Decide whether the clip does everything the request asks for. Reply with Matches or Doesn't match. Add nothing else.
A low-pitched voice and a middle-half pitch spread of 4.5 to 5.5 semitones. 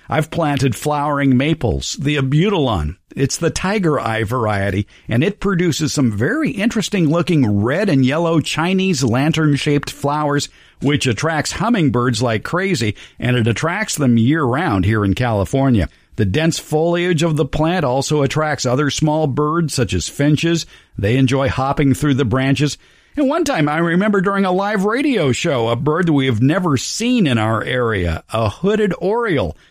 Doesn't match